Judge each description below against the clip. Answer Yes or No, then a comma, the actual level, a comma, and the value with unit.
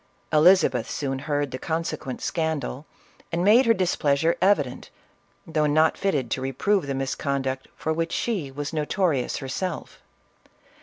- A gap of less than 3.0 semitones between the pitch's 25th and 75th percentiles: No, average, 4.1 semitones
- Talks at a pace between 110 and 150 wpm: Yes, average, 140 wpm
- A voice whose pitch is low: No, medium, 150 Hz